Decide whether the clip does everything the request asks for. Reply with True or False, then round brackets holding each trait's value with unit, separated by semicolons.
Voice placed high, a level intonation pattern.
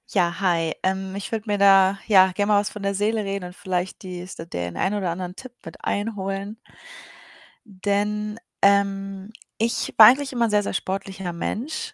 True (195 Hz; 1.9 semitones)